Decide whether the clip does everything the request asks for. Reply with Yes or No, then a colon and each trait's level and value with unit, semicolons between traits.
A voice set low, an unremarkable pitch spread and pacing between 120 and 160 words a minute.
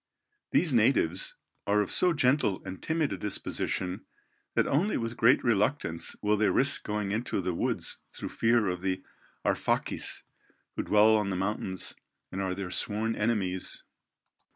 Yes: low, 105 Hz; average, 3.8 semitones; average, 150 wpm